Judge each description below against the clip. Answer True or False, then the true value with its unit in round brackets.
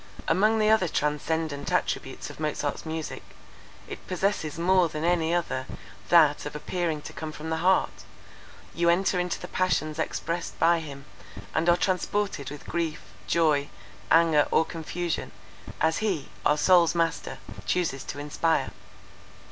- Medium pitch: True (165 Hz)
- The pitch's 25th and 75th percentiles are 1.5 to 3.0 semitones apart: True (2.6 semitones)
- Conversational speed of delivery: True (145 wpm)